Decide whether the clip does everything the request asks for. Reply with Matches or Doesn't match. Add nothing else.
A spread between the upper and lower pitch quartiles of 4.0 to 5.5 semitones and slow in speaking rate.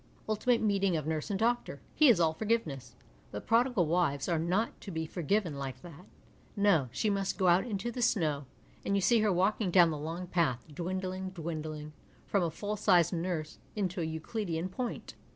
Doesn't match